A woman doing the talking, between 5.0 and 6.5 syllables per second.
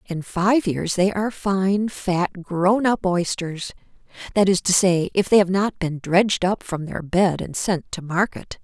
No: female; 4.1 syllables/s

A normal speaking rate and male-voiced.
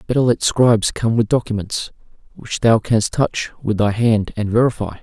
Yes: average, 180 wpm; male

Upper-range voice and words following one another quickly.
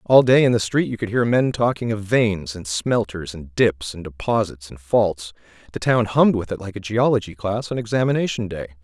No: low, 105 Hz; fast, 210 wpm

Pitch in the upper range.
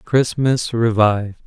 No: low, 115 Hz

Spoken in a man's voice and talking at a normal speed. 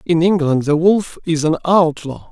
Yes: male; average, 180 wpm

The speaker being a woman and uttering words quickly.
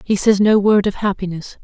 Yes: female; fast, 220 wpm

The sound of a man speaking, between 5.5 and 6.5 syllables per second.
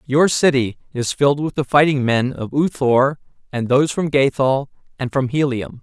No: male; 4.9 syllables/s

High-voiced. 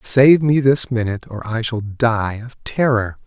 No: low, 120 Hz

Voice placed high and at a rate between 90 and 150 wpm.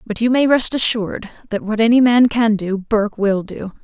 No: high, 220 Hz; fast, 220 wpm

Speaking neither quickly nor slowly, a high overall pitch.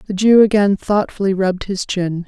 Yes: average, 185 wpm; high, 195 Hz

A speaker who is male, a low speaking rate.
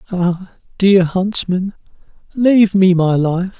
Yes: male; slow, 115 wpm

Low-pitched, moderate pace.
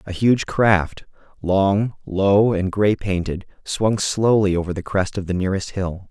Yes: low, 100 Hz; average, 165 wpm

